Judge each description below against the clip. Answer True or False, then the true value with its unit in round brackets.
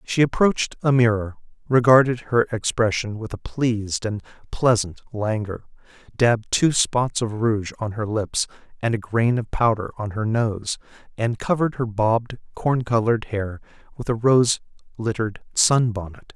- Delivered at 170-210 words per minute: False (150 wpm)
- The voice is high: False (115 Hz)